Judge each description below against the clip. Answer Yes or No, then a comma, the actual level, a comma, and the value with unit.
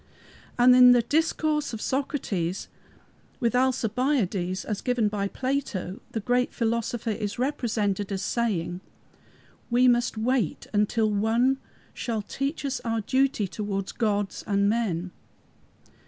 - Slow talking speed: Yes, slow, 125 wpm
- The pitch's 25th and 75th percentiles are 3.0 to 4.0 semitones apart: Yes, average, 3.7 semitones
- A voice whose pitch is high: Yes, high, 230 Hz